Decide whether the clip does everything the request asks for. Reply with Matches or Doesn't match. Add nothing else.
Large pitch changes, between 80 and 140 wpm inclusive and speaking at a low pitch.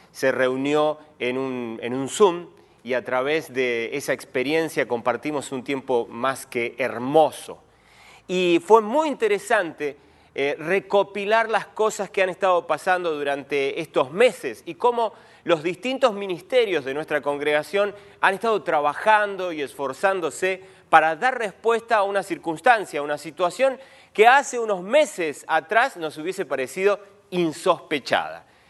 Doesn't match